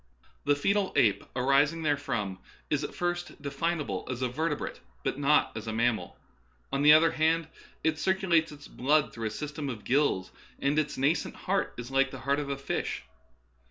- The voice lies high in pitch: No, medium, 145 Hz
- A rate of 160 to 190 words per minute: Yes, average, 185 wpm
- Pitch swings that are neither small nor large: Yes, average, 3.4 semitones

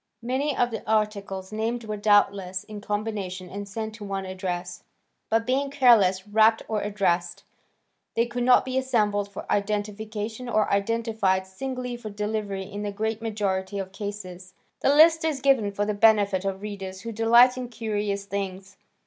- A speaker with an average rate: Yes, average, 165 wpm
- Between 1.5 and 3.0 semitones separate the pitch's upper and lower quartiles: Yes, narrow, 2.6 semitones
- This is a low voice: No, high, 210 Hz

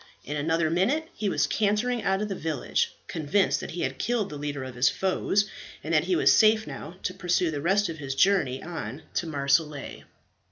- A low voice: No, medium, 170 Hz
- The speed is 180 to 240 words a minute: Yes, fast, 205 wpm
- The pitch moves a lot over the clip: Yes, wide, 5.8 semitones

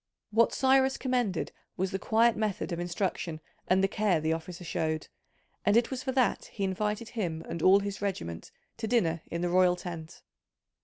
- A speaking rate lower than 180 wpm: No, average, 185 wpm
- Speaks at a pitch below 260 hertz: Yes, high, 190 Hz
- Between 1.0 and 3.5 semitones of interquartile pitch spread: No, average, 4.7 semitones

